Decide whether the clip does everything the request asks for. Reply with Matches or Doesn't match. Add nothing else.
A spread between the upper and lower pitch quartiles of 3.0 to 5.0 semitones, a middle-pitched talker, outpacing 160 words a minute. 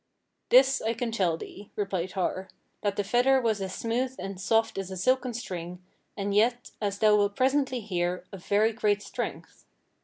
Doesn't match